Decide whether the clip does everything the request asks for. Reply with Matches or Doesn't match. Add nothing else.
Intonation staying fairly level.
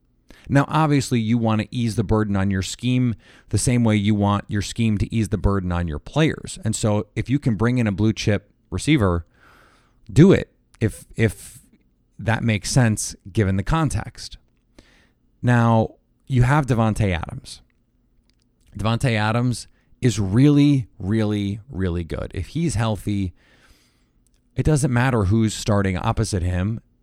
Doesn't match